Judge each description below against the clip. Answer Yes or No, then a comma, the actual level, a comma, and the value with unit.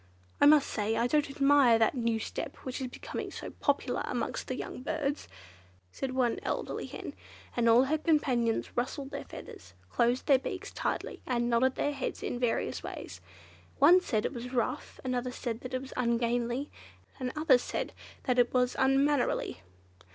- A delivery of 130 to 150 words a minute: No, average, 165 wpm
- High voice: Yes, very high, 255 Hz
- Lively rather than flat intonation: No, narrow, 2.6 semitones